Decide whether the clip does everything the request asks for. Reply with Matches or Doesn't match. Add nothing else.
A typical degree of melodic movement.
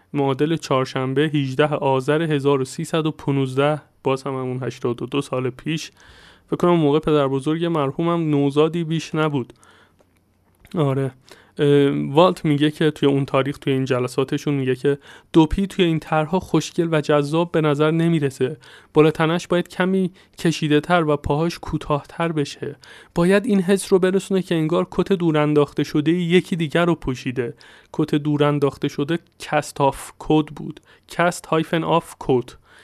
Matches